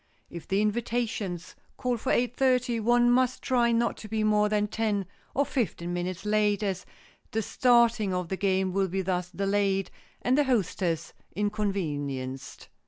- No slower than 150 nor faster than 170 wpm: Yes, average, 160 wpm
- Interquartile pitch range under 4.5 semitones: Yes, average, 4.0 semitones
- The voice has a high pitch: Yes, high, 210 Hz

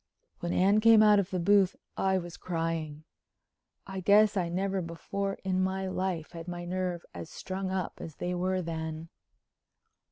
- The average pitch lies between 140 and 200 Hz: Yes, medium, 185 Hz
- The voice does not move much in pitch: Yes, narrow, 2.3 semitones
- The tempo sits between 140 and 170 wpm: Yes, average, 165 wpm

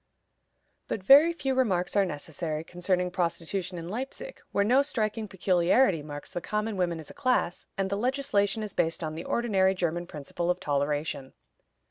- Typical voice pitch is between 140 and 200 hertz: Yes, medium, 185 Hz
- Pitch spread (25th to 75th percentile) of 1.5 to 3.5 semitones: No, average, 4.3 semitones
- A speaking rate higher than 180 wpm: No, average, 165 wpm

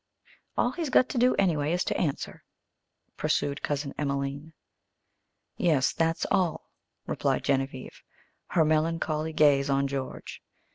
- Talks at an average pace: No, slow, 125 wpm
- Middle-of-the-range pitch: Yes, medium, 155 Hz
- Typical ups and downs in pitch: Yes, average, 3.1 semitones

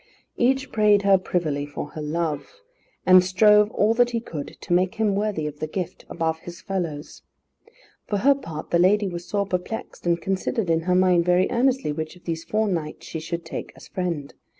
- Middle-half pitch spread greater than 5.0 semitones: No, average, 4.3 semitones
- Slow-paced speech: No, average, 195 wpm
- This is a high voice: No, medium, 180 Hz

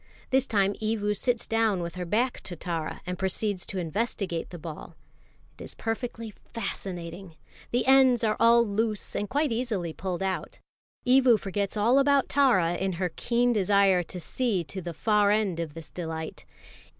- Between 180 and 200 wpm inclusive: No, average, 170 wpm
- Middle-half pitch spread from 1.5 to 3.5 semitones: No, average, 4.6 semitones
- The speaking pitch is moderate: No, high, 205 Hz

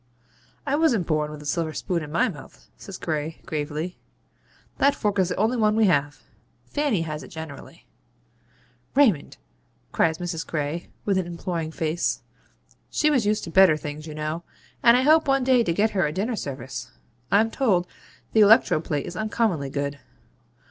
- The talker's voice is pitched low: No, medium, 175 Hz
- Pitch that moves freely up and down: Yes, wide, 6.0 semitones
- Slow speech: No, average, 175 wpm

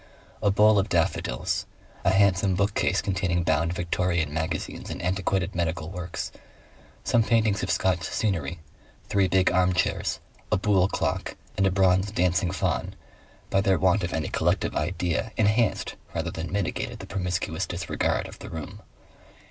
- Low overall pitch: Yes, very low, 90 Hz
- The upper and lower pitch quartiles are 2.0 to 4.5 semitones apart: Yes, narrow, 2.4 semitones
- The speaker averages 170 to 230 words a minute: No, average, 150 wpm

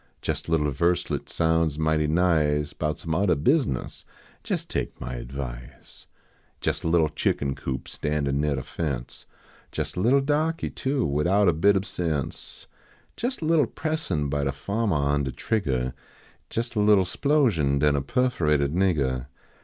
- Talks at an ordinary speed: Yes, average, 160 wpm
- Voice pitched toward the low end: Yes, very low, 80 Hz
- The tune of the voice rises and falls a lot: Yes, wide, 6.4 semitones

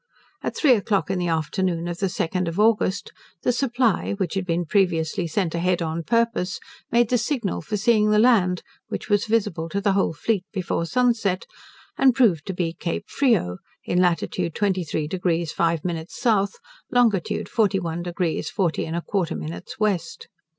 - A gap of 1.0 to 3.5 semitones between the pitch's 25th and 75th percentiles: No, average, 4.0 semitones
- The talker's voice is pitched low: No, medium, 185 Hz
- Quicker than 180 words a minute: No, average, 170 wpm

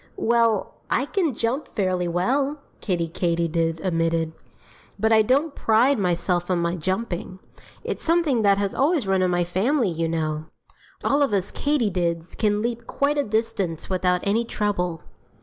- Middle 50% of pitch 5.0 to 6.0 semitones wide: Yes, average, 5.3 semitones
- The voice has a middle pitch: No, high, 195 Hz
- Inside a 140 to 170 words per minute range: Yes, average, 155 wpm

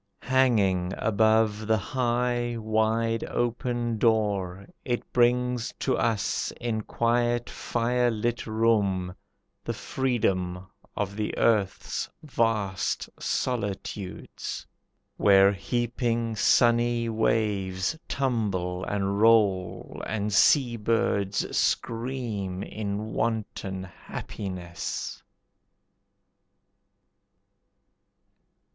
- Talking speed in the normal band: No, slow, 75 wpm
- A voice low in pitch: Yes, low, 110 Hz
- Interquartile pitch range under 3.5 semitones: Yes, average, 3.1 semitones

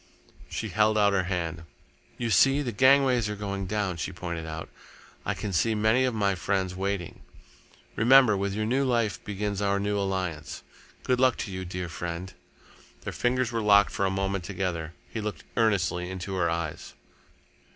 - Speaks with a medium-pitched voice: No, low, 100 Hz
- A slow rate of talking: No, average, 175 wpm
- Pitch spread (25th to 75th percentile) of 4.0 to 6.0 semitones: No, average, 3.3 semitones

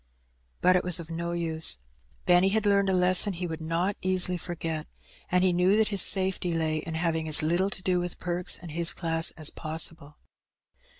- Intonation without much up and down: Yes, narrow, 2.2 semitones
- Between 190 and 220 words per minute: Yes, average, 195 wpm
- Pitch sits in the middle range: Yes, medium, 175 Hz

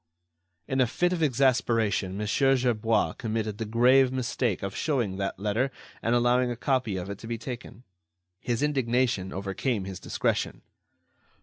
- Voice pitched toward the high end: No, low, 115 Hz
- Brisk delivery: No, average, 150 wpm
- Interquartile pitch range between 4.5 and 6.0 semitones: No, average, 3.7 semitones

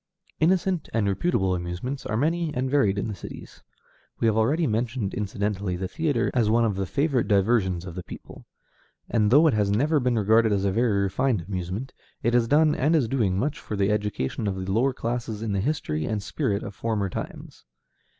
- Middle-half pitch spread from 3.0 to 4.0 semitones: No, average, 4.8 semitones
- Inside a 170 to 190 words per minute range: No, average, 200 wpm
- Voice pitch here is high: No, low, 110 Hz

